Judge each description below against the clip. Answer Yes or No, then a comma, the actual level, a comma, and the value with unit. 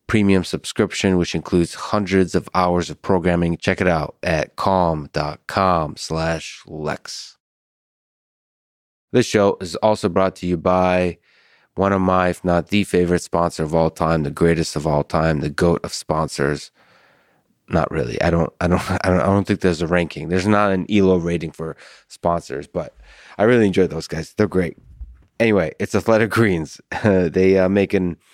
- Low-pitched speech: Yes, very low, 90 Hz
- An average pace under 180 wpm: Yes, average, 170 wpm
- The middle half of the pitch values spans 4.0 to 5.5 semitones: No, average, 2.9 semitones